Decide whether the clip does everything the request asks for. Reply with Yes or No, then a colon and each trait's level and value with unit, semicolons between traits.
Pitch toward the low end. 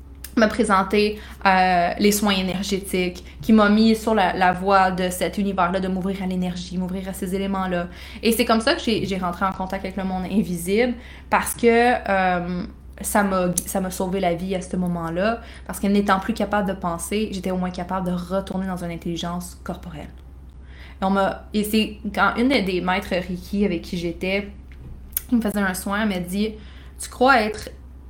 No: high, 190 Hz